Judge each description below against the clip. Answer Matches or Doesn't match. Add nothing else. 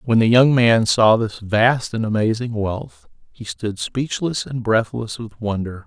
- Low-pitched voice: Matches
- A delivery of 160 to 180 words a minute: Matches